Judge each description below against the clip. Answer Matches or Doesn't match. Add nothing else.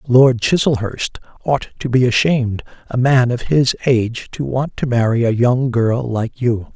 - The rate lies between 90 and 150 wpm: Doesn't match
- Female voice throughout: Doesn't match